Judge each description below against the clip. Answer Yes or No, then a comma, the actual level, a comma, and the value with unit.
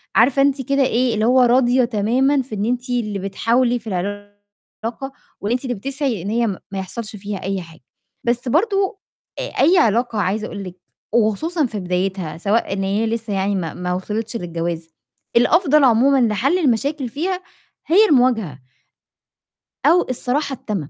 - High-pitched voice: Yes, high, 230 Hz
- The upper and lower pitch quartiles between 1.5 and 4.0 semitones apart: No, average, 4.8 semitones